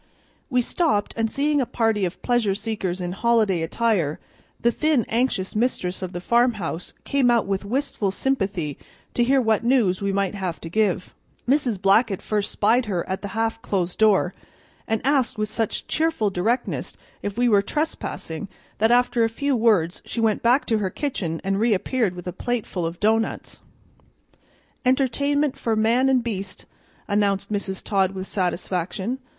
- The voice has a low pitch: No, high, 215 Hz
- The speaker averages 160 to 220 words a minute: Yes, average, 165 wpm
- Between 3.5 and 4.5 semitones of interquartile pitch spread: Yes, average, 4.1 semitones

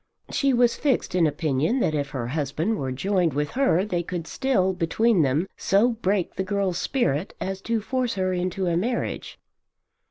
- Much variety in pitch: Yes, wide, 5.8 semitones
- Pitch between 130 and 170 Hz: No, medium, 185 Hz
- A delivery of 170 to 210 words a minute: Yes, average, 180 wpm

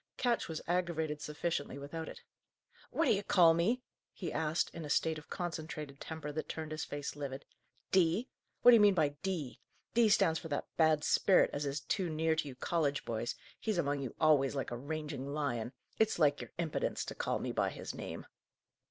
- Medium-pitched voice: Yes, medium, 155 Hz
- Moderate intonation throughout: Yes, average, 3.1 semitones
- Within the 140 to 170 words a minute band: No, average, 195 wpm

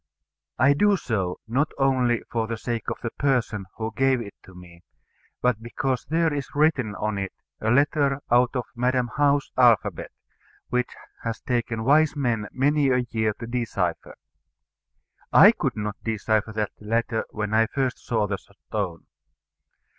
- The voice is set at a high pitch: No, low, 120 Hz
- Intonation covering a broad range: No, average, 3.8 semitones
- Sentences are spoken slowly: No, average, 155 wpm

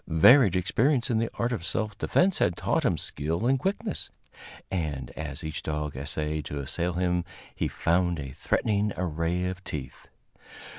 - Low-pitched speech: Yes, very low, 90 Hz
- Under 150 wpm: No, average, 160 wpm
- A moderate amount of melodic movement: No, wide, 5.9 semitones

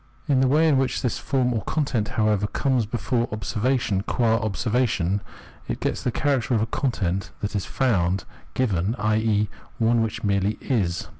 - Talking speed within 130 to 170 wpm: Yes, average, 165 wpm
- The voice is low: Yes, low, 110 Hz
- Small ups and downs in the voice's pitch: No, average, 3.6 semitones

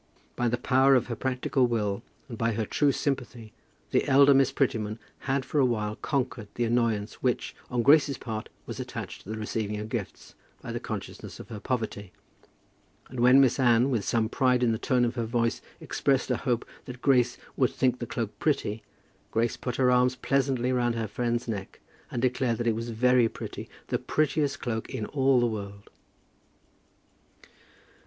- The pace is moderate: Yes, average, 185 wpm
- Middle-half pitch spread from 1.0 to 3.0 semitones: Yes, narrow, 2.5 semitones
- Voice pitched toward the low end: Yes, low, 120 Hz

